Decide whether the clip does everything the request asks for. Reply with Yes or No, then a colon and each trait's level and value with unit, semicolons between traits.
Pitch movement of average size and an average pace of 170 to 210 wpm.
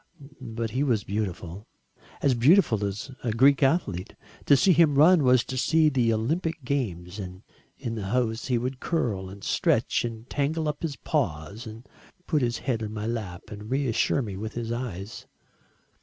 Yes: average, 4.7 semitones; average, 175 wpm